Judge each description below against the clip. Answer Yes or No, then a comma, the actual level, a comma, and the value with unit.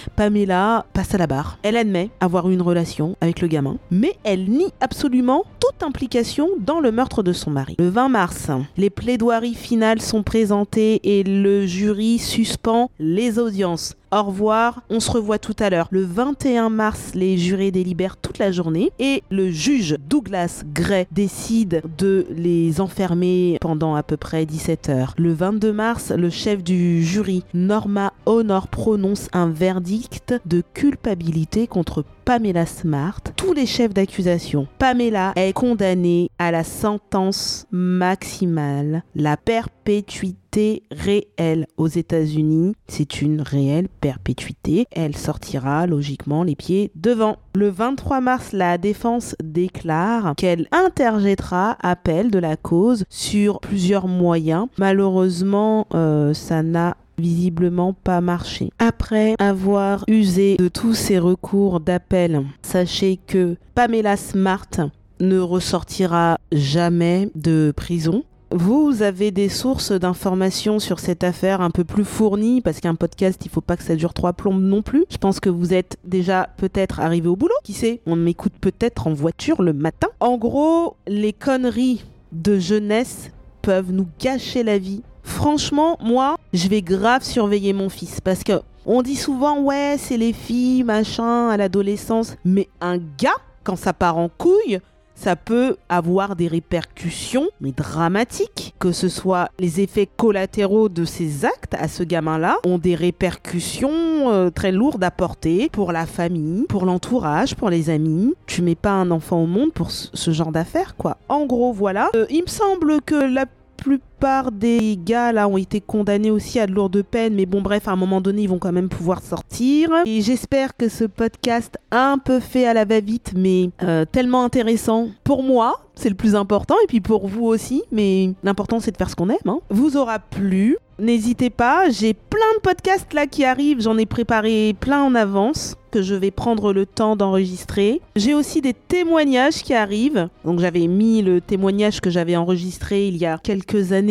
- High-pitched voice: Yes, high, 195 Hz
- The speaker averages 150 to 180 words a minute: Yes, average, 165 wpm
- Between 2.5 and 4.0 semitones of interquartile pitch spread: No, average, 4.6 semitones